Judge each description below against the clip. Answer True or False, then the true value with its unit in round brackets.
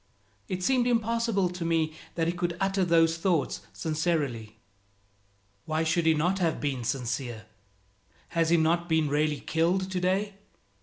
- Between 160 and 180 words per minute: False (145 wpm)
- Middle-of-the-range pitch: True (165 Hz)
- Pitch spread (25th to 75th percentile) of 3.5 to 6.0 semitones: False (3.0 semitones)